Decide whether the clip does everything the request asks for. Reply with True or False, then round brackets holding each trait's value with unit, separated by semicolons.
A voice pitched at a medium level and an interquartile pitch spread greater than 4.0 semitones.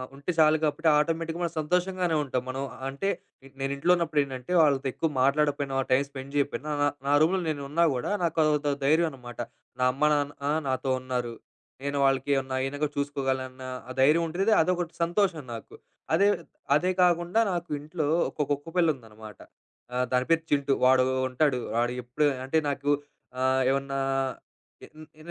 False (145 Hz; 3.6 semitones)